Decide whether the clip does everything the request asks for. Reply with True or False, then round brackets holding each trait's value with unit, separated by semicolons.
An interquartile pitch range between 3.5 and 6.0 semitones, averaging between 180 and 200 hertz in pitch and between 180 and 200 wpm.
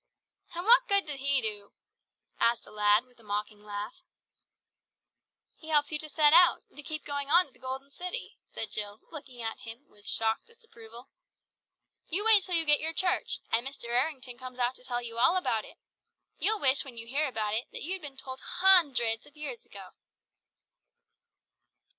False (5.6 semitones; 265 Hz; 185 wpm)